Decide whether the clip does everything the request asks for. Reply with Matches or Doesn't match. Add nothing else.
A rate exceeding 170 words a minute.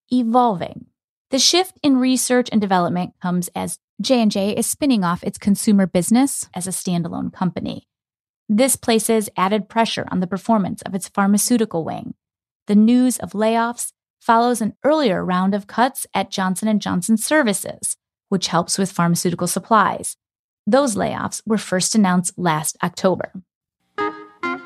Doesn't match